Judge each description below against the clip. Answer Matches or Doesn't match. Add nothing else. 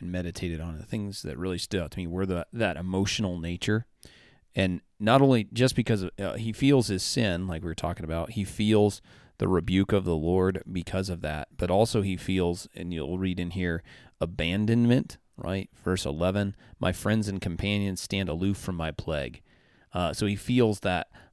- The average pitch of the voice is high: Doesn't match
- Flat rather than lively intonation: Doesn't match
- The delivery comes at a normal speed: Matches